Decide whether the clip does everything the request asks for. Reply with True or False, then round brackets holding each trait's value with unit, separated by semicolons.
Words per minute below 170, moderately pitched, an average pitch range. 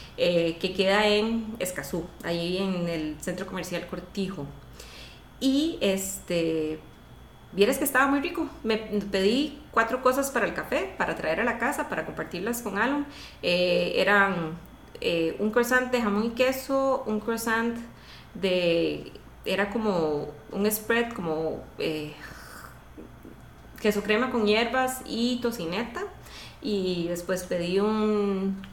False (130 wpm; 200 Hz; 4.9 semitones)